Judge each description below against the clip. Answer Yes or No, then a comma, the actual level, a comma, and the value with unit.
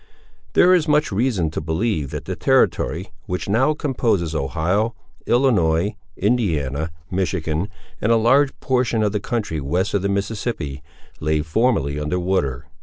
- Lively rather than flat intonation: Yes, wide, 6.8 semitones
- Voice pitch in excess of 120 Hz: No, low, 100 Hz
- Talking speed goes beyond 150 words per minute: No, average, 145 wpm